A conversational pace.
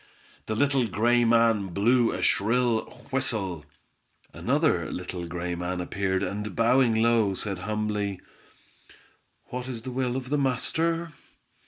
No: slow, 130 wpm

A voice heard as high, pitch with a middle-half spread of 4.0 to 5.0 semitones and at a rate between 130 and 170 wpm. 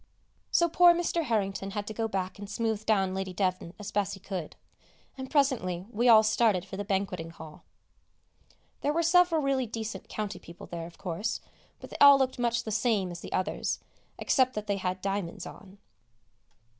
No: high, 205 Hz; average, 4.3 semitones; average, 185 wpm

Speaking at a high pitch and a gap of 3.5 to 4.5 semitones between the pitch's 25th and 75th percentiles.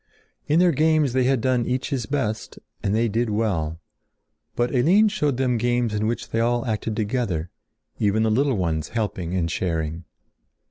No: low, 115 Hz; average, 4.1 semitones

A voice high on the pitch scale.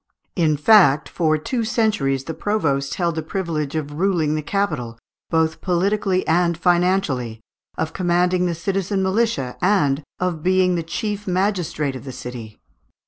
No: medium, 170 Hz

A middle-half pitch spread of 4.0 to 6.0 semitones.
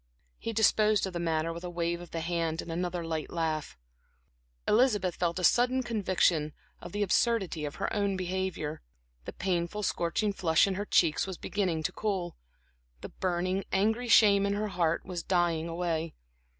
No: average, 3.3 semitones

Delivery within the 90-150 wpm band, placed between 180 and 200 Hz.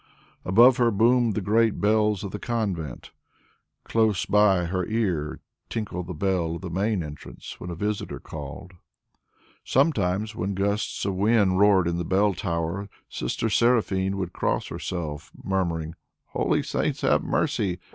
No: average, 145 wpm; very low, 95 Hz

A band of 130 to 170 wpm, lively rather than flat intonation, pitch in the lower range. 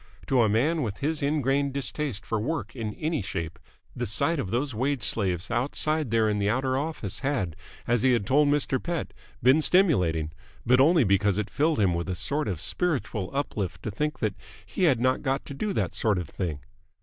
No: fast, 205 wpm; wide, 6.2 semitones; low, 125 Hz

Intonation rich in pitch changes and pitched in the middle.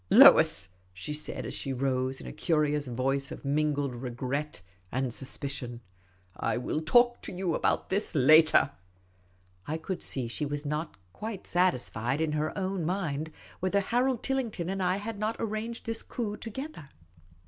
Yes: wide, 6.5 semitones; medium, 155 Hz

